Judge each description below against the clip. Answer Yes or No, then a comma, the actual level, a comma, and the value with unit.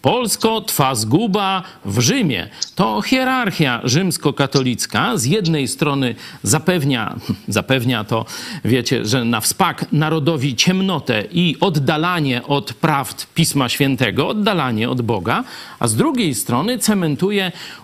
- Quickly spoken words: No, average, 115 wpm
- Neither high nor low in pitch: Yes, medium, 150 Hz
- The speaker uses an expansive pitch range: Yes, wide, 6.1 semitones